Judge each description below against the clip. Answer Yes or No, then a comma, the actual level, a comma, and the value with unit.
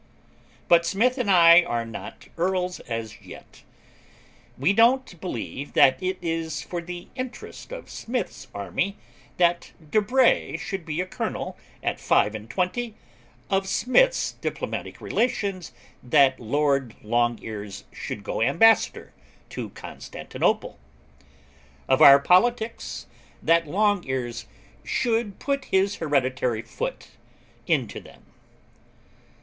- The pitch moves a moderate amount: No, wide, 7.7 semitones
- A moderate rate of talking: No, slow, 115 wpm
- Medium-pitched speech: Yes, medium, 175 Hz